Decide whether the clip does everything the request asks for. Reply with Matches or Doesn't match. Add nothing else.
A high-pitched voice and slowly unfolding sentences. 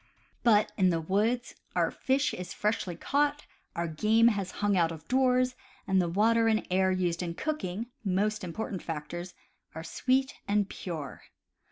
Doesn't match